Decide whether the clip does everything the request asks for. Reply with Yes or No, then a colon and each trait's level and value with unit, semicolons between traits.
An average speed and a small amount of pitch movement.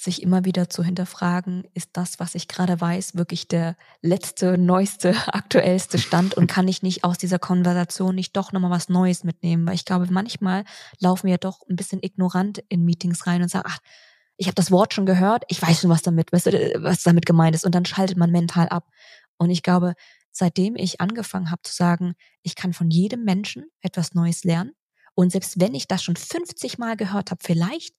No: fast, 205 wpm; narrow, 1.4 semitones